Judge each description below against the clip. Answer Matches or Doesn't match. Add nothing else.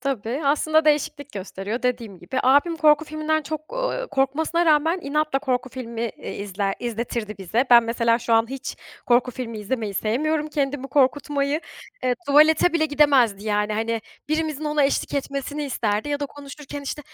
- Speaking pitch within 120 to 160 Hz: Doesn't match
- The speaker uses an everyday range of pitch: Matches